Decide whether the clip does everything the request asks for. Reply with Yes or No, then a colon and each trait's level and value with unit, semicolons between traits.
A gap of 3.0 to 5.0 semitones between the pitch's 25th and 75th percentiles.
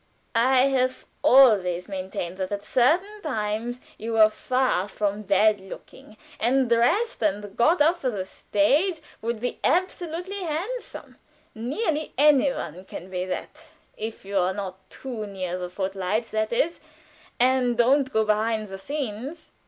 No: wide, 5.4 semitones